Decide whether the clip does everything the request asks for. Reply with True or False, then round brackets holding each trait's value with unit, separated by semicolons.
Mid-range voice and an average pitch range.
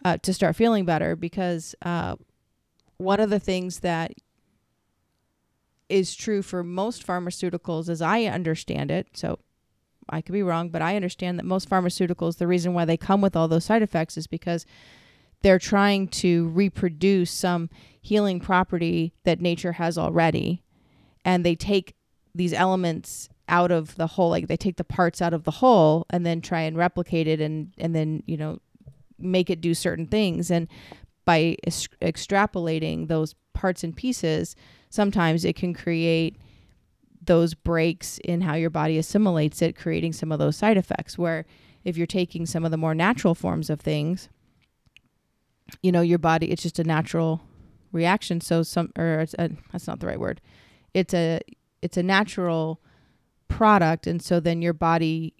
False (170 Hz; 2.0 semitones)